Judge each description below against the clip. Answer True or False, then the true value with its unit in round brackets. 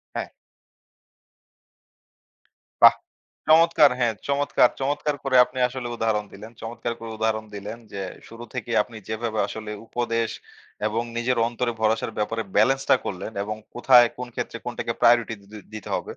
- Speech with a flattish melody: True (2.3 semitones)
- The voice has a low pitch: True (115 Hz)